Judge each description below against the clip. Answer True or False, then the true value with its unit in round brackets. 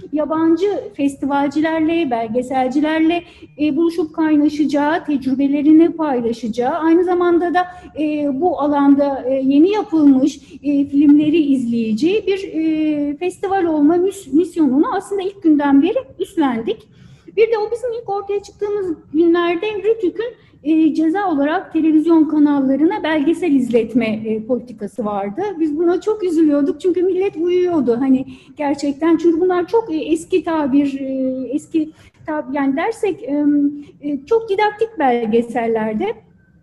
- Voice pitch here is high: True (315 Hz)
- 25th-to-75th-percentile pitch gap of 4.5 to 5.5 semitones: False (4.1 semitones)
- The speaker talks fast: False (125 wpm)